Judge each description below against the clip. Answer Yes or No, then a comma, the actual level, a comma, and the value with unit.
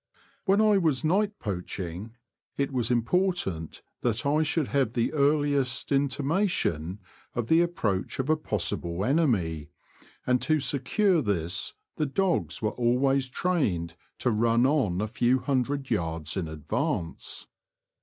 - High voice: No, low, 125 Hz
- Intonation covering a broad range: Yes, wide, 7.6 semitones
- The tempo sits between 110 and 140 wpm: Yes, slow, 135 wpm